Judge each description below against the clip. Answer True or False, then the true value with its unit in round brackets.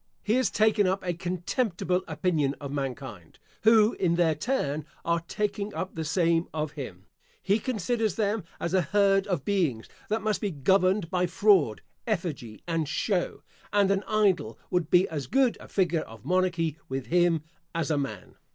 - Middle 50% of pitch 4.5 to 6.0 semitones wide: True (4.8 semitones)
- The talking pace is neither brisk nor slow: True (170 wpm)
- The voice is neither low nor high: True (175 Hz)